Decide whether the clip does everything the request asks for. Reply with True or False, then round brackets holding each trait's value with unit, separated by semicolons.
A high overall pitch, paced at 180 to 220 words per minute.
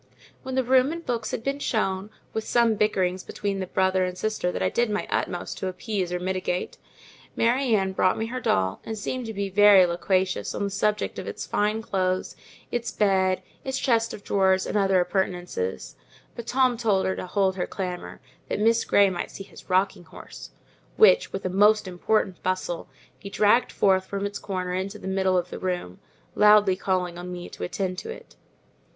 True (195 Hz; 195 wpm)